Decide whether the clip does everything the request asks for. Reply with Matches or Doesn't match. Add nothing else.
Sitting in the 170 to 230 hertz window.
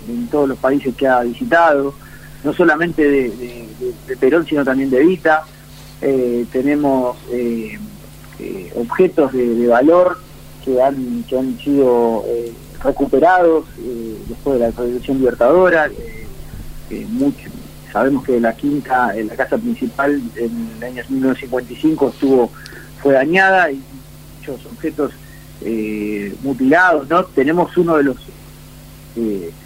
Doesn't match